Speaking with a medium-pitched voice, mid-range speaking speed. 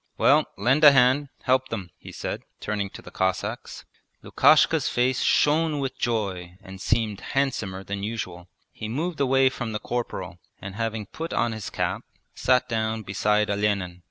No: low, 110 Hz; average, 160 wpm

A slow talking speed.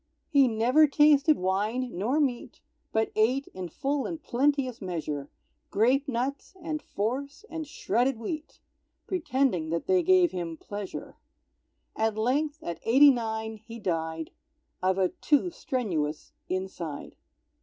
Yes: slow, 130 wpm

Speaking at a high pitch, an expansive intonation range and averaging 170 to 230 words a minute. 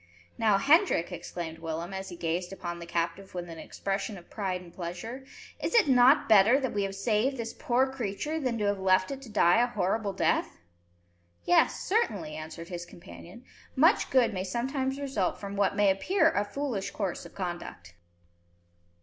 Yes: high, 200 Hz; wide, 5.9 semitones; average, 180 wpm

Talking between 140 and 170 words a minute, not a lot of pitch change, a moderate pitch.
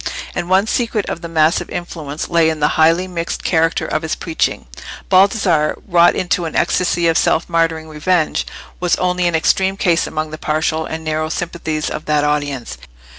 No: average, 180 wpm; narrow, 2.2 semitones; medium, 165 Hz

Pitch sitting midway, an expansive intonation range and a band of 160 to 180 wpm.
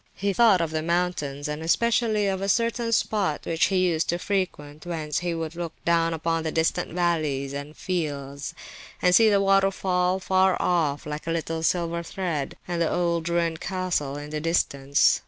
No: medium, 170 Hz; average, 3.2 semitones; average, 175 wpm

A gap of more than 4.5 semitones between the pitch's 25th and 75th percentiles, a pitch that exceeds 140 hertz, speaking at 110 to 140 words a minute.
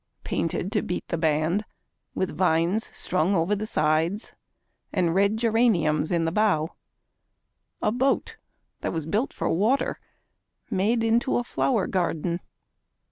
Yes: average, 5.1 semitones; high, 190 Hz; slow, 135 wpm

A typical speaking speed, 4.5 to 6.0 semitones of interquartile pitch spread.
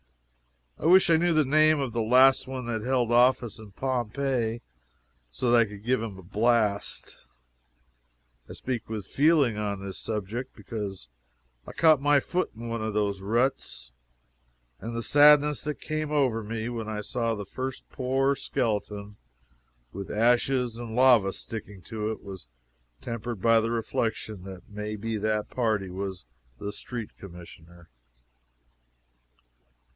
No: average, 150 wpm; average, 3.8 semitones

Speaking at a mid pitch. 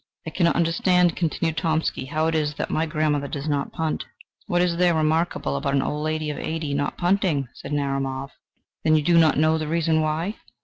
Yes: medium, 155 Hz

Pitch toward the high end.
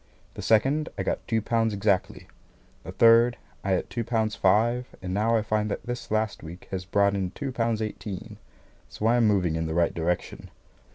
No: low, 110 Hz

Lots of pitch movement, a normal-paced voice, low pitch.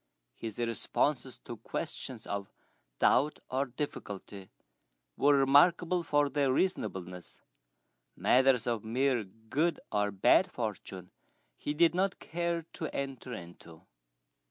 No: wide, 6.3 semitones; slow, 110 wpm; low, 130 Hz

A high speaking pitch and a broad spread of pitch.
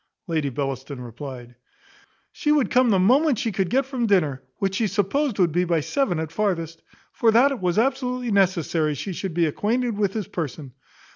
Yes: high, 195 Hz; wide, 6.9 semitones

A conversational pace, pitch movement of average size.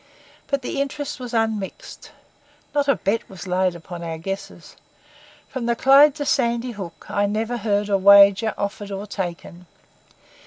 Yes: average, 155 wpm; average, 4.0 semitones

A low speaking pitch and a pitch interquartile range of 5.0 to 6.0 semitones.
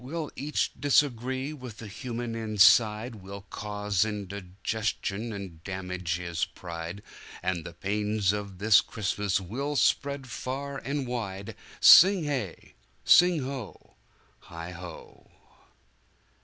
Yes: low, 105 Hz; wide, 5.4 semitones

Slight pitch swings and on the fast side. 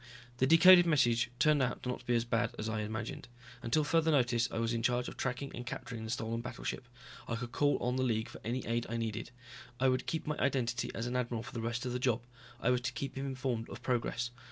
Yes: narrow, 2.1 semitones; fast, 250 wpm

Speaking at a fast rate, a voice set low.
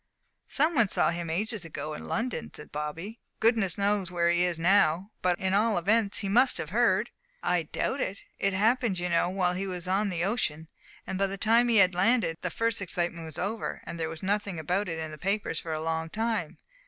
No: fast, 220 wpm; high, 190 Hz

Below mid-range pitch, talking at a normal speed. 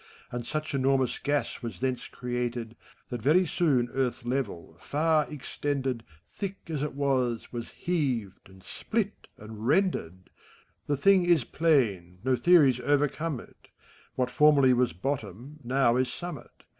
Yes: low, 130 Hz; average, 145 wpm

